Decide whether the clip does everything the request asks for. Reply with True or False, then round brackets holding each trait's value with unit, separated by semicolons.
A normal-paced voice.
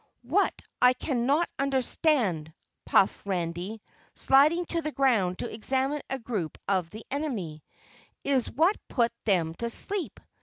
False (130 wpm)